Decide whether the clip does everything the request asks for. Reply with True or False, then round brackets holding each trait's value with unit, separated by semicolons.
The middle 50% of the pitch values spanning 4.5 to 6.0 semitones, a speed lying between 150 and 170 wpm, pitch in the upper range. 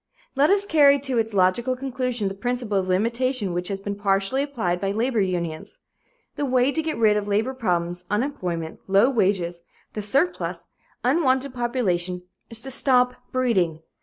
True (5.4 semitones; 165 wpm; 225 Hz)